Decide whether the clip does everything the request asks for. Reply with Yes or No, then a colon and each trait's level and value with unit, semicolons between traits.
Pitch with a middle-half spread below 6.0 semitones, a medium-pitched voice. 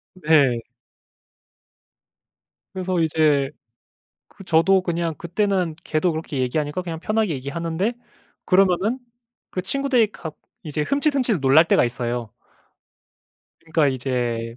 Yes: average, 5.1 semitones; medium, 165 Hz